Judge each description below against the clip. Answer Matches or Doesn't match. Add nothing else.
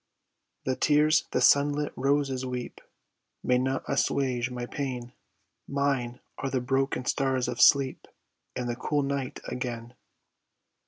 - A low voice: Matches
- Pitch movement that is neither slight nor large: Doesn't match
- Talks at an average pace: Doesn't match